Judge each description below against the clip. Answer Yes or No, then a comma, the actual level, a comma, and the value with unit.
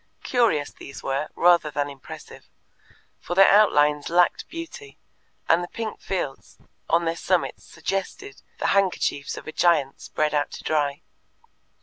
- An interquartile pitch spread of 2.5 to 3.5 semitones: No, average, 4.8 semitones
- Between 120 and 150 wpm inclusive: Yes, average, 140 wpm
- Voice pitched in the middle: Yes, medium, 170 Hz